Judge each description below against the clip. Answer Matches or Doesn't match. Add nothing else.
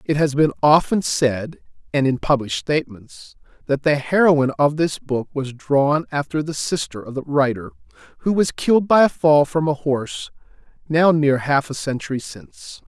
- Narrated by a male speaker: Matches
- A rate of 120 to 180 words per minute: Matches